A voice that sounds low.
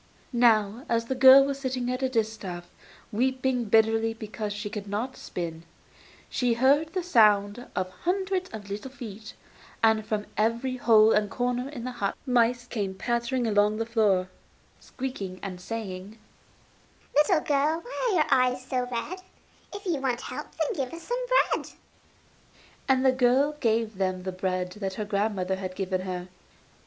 No: high, 230 Hz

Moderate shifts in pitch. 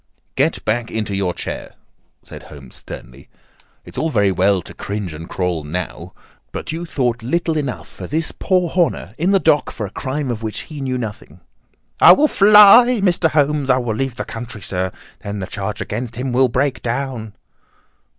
No: wide, 7.0 semitones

